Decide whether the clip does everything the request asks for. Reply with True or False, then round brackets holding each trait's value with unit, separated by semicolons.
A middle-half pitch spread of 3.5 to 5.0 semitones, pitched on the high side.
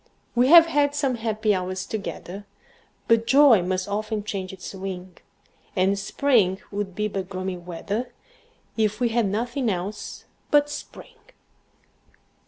True (4.0 semitones; 210 Hz)